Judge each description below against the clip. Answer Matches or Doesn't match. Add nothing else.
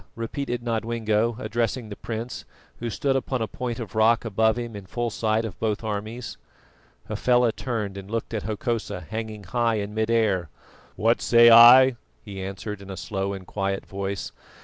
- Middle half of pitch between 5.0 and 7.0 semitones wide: Doesn't match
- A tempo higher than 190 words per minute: Doesn't match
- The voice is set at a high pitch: Doesn't match